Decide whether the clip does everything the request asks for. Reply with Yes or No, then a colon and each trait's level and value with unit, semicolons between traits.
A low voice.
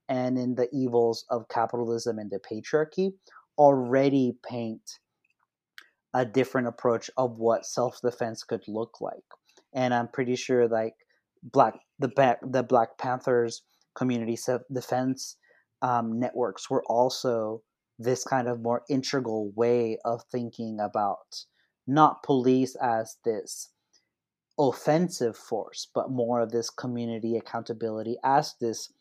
Yes: low, 120 Hz